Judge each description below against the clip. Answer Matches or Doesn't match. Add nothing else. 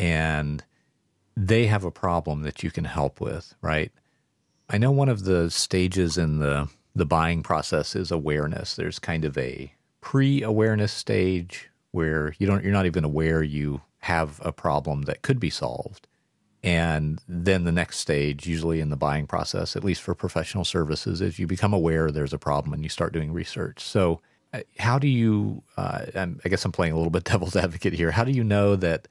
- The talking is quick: Doesn't match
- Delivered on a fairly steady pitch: Doesn't match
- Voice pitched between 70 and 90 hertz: Matches